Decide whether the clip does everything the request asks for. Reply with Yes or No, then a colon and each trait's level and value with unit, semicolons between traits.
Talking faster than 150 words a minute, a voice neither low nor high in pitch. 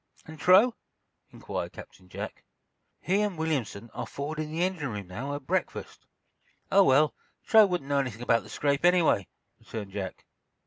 Yes: average, 165 wpm; medium, 145 Hz